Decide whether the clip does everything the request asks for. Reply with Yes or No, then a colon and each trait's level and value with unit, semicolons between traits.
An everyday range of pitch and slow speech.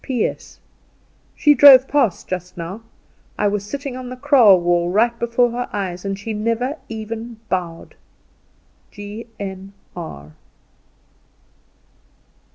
Yes: average, 4.5 semitones; slow, 110 wpm